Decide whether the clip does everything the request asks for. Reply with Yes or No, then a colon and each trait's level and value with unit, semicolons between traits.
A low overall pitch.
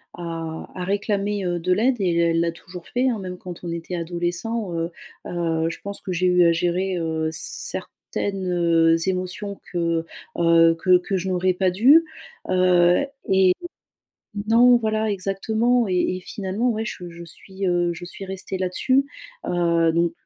No: medium, 180 Hz